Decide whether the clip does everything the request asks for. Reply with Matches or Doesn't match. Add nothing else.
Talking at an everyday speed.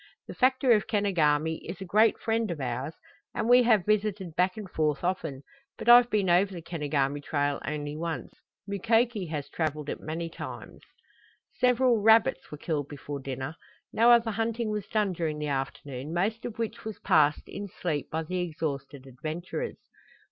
Matches